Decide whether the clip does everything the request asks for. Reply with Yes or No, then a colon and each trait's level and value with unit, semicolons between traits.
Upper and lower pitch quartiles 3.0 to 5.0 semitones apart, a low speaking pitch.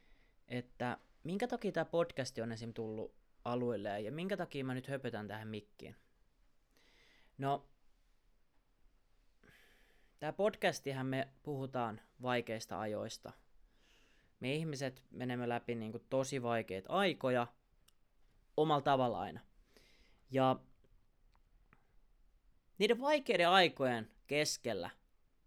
Yes: average, 4.0 semitones; low, 130 Hz